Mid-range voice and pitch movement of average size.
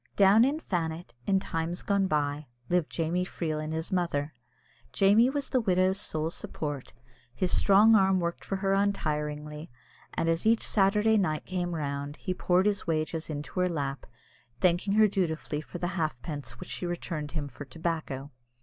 Yes: medium, 170 Hz; average, 4.1 semitones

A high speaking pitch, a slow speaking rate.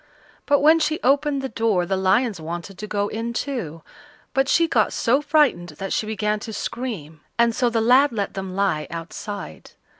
No: high, 220 Hz; average, 185 wpm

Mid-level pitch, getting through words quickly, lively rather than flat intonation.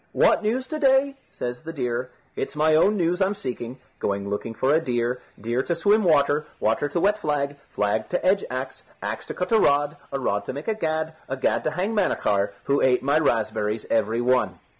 Yes: medium, 145 Hz; fast, 210 wpm; wide, 6.7 semitones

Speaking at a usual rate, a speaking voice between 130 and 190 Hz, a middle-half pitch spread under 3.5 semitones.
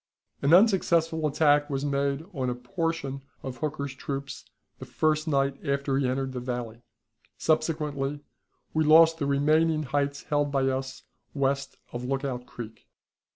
Yes: average, 145 wpm; medium, 140 Hz; narrow, 2.4 semitones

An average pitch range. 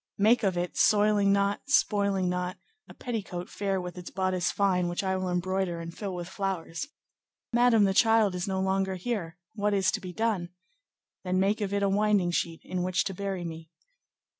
No: narrow, 2.3 semitones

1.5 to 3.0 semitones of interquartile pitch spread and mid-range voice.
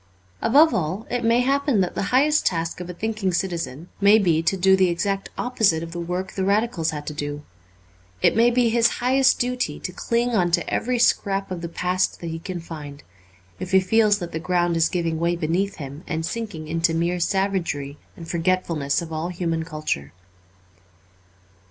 No: average, 4.4 semitones; medium, 180 Hz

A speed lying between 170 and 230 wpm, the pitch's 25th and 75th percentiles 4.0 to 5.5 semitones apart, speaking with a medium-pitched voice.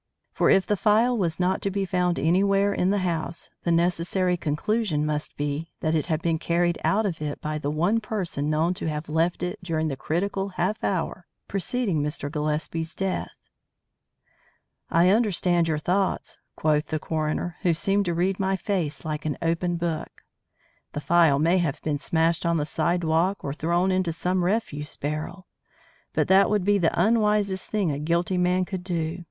No: average, 180 wpm; average, 3.3 semitones; medium, 175 Hz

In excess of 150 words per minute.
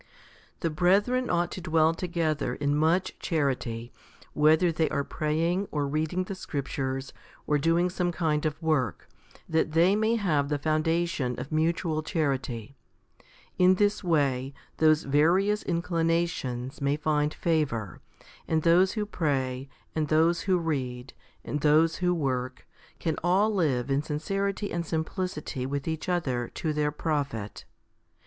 No: average, 140 wpm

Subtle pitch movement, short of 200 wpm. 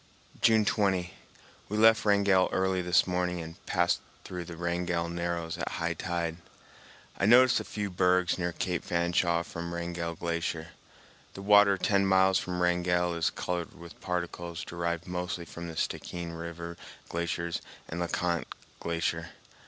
Yes: narrow, 1.4 semitones; average, 150 wpm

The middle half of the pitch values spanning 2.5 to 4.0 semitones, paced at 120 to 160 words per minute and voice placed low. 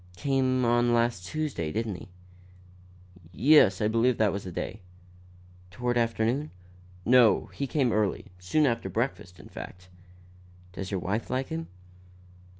No: average, 4.8 semitones; average, 140 wpm; low, 115 Hz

